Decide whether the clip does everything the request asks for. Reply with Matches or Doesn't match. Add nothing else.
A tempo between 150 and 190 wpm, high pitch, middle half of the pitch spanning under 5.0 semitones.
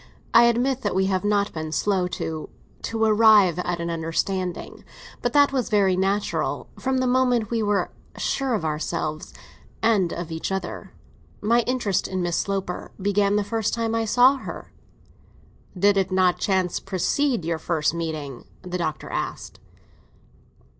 Matches